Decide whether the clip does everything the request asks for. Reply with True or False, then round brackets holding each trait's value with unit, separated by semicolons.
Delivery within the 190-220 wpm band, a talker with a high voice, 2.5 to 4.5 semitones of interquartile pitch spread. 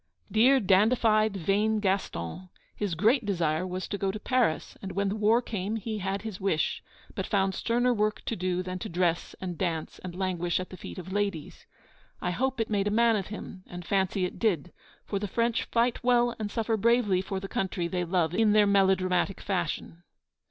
True (200 wpm; 195 Hz; 3.0 semitones)